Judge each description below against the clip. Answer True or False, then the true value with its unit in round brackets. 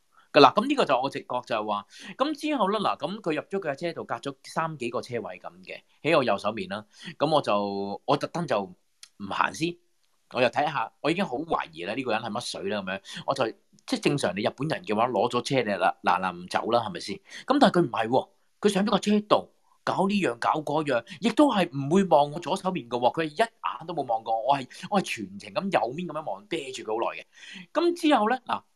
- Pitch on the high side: False (175 Hz)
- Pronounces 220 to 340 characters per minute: True (330 characters per minute)